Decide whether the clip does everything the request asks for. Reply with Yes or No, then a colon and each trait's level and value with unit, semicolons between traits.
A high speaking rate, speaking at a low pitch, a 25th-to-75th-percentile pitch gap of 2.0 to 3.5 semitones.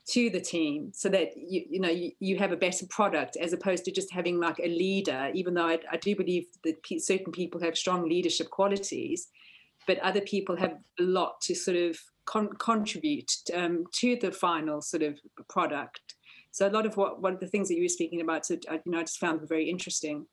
No: fast, 220 wpm; medium, 180 Hz; narrow, 2.6 semitones